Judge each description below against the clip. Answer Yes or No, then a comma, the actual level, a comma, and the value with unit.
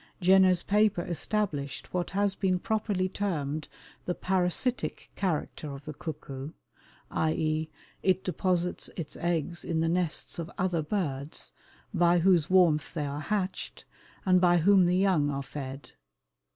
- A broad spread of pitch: No, average, 3.5 semitones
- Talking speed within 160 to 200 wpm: No, average, 140 wpm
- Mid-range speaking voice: Yes, medium, 175 Hz